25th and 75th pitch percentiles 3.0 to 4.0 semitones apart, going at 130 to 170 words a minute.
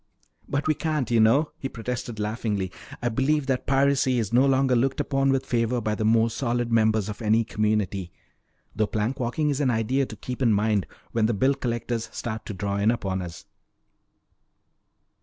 No: average, 3.6 semitones; average, 185 wpm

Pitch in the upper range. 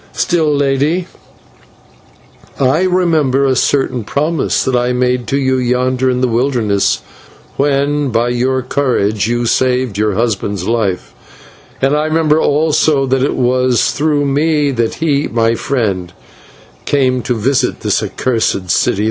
No: low, 130 Hz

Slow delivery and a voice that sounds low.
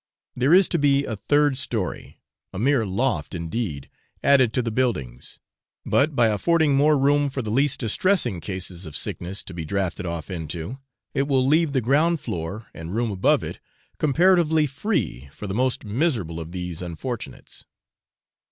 No: average, 165 wpm; low, 120 Hz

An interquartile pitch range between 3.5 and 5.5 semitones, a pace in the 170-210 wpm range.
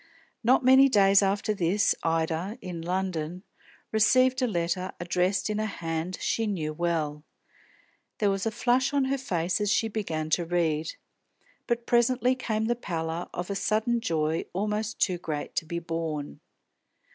No: average, 5.0 semitones; average, 160 wpm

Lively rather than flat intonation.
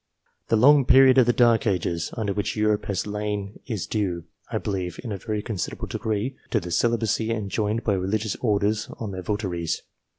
No: narrow, 2.4 semitones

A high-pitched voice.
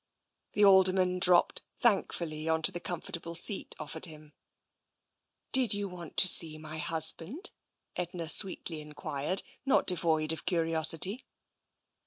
No: medium, 170 Hz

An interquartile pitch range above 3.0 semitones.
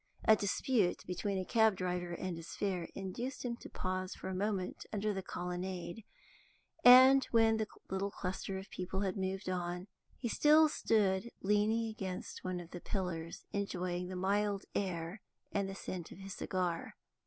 No: narrow, 2.6 semitones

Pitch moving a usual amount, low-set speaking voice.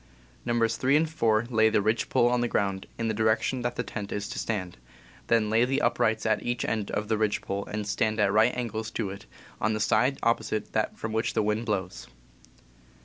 No: narrow, 1.9 semitones; low, 110 Hz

